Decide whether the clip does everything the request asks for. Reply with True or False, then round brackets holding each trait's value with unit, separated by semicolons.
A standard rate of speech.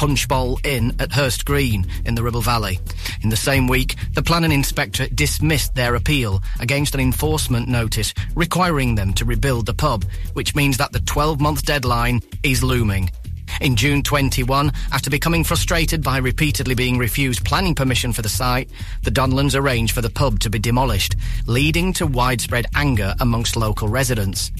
True (165 wpm)